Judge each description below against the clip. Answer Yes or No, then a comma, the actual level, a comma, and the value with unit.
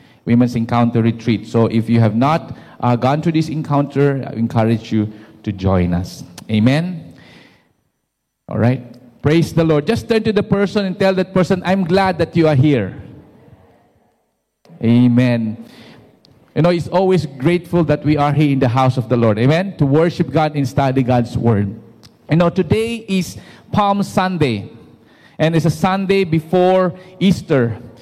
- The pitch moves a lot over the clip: Yes, wide, 6.9 semitones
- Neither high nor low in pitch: Yes, medium, 145 Hz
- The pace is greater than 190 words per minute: No, average, 165 wpm